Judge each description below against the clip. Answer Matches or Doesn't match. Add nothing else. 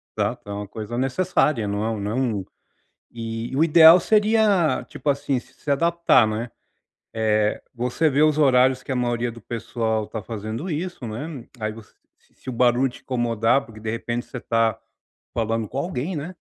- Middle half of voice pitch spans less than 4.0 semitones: Doesn't match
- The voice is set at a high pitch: Doesn't match